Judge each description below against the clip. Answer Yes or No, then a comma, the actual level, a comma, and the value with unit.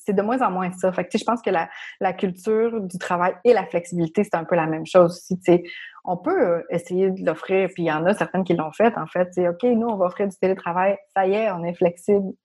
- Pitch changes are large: No, average, 2.9 semitones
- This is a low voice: No, medium, 185 Hz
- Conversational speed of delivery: No, fast, 270 wpm